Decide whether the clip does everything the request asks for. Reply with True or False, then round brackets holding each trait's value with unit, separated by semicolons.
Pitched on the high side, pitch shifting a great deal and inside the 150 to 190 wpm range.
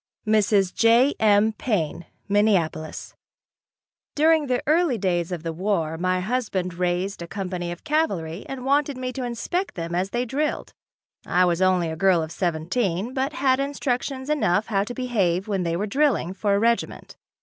True (205 Hz; 6.3 semitones; 170 wpm)